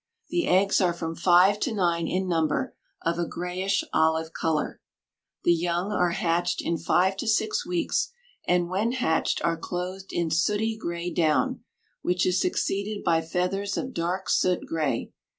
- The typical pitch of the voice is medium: Yes, medium, 180 Hz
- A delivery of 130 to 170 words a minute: Yes, average, 160 wpm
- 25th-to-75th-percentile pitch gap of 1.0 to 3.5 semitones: Yes, average, 2.8 semitones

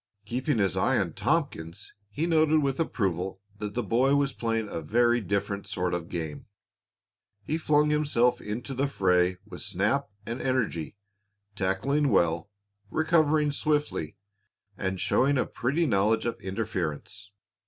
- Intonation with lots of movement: Yes, wide, 6.9 semitones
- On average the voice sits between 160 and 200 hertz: No, low, 115 Hz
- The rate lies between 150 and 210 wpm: No, average, 140 wpm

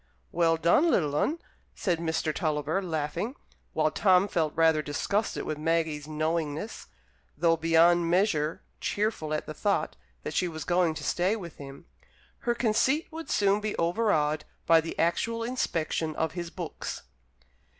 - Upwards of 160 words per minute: No, average, 150 wpm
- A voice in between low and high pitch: Yes, medium, 165 Hz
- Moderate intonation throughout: Yes, average, 4.2 semitones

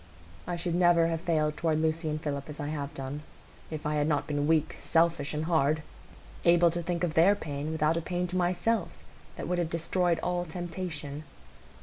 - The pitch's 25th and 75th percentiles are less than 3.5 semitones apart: Yes, narrow, 2.4 semitones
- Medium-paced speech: Yes, average, 195 wpm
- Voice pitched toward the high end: No, medium, 160 Hz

